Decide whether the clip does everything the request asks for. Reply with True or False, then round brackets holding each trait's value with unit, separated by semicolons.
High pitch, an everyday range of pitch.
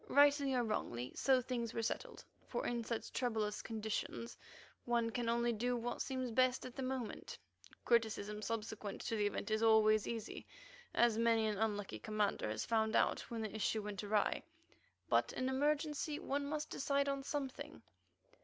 True (230 Hz; 3.0 semitones)